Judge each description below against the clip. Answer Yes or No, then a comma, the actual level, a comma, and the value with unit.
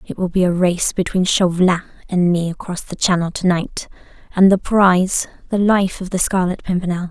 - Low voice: No, medium, 180 Hz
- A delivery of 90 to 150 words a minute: No, average, 175 wpm